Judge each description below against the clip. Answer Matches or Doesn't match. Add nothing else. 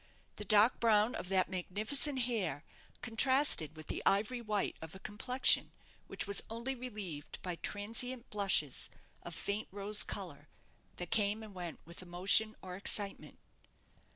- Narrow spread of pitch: Doesn't match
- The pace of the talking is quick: Doesn't match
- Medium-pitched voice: Doesn't match